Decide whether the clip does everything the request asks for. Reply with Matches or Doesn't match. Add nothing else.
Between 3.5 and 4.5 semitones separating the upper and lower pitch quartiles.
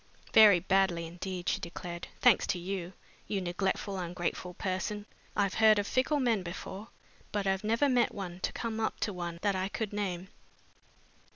Doesn't match